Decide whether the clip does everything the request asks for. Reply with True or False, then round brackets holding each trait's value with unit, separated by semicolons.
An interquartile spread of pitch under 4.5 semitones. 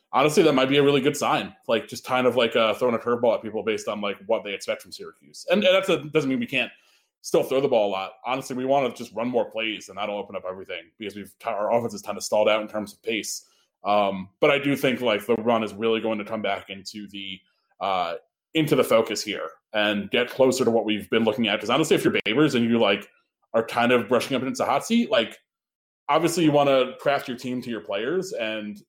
False (4.9 semitones)